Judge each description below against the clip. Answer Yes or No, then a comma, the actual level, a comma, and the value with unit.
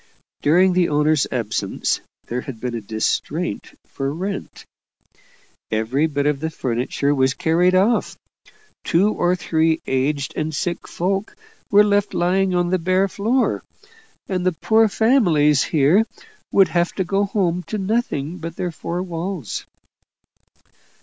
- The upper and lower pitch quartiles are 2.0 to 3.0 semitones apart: No, average, 4.7 semitones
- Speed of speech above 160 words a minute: No, average, 140 wpm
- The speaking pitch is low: No, medium, 175 Hz